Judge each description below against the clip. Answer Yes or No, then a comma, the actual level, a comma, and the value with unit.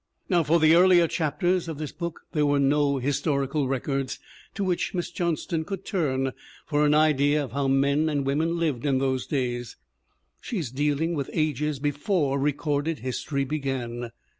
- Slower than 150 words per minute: No, average, 165 wpm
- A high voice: No, medium, 145 Hz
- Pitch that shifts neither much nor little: Yes, average, 3.0 semitones